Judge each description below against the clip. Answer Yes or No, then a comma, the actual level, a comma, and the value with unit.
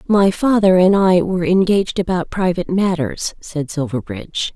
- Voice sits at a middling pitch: Yes, medium, 180 Hz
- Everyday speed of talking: Yes, average, 145 wpm